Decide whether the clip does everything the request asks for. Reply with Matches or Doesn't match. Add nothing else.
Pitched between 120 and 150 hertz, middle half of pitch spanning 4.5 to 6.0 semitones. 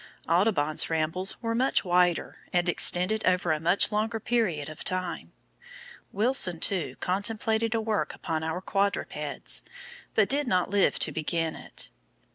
Doesn't match